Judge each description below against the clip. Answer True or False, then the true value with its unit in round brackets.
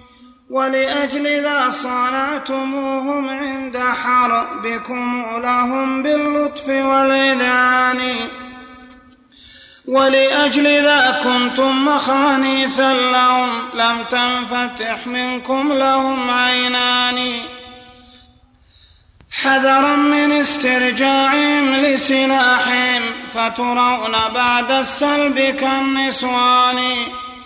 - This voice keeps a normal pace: False (55 wpm)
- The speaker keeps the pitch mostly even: True (1.4 semitones)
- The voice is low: False (255 Hz)